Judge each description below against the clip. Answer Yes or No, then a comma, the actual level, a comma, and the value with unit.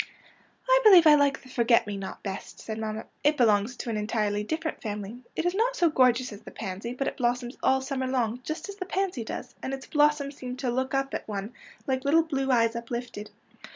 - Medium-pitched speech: No, very high, 255 Hz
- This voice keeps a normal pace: No, fast, 240 wpm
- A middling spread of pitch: Yes, average, 4.5 semitones